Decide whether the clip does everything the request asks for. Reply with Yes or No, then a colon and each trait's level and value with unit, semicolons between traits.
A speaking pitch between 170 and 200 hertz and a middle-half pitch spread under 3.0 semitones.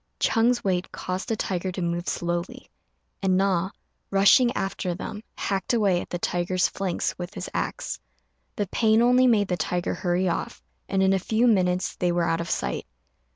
Yes: medium, 185 Hz; narrow, 2.6 semitones